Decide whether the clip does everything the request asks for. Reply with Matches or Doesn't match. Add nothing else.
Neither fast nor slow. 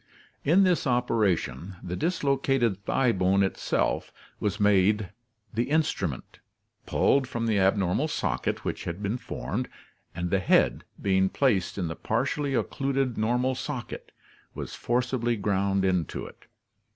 Doesn't match